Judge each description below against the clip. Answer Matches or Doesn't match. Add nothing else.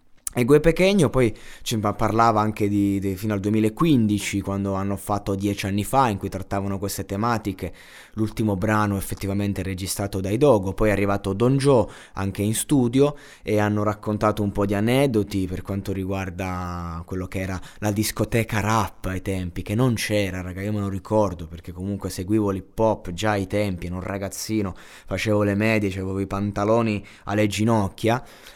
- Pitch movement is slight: Matches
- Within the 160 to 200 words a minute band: Matches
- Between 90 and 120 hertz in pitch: Matches